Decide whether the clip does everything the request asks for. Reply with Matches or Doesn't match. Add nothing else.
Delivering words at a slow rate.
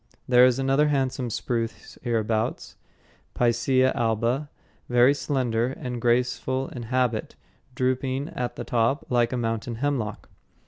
Matches